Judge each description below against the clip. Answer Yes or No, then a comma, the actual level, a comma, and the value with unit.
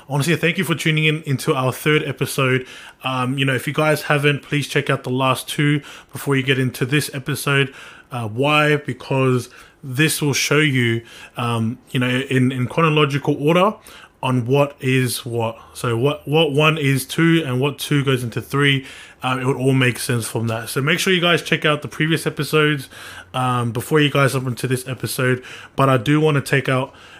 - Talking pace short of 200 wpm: No, fast, 205 wpm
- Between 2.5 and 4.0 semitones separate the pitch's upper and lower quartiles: Yes, average, 2.8 semitones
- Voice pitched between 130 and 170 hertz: Yes, medium, 140 Hz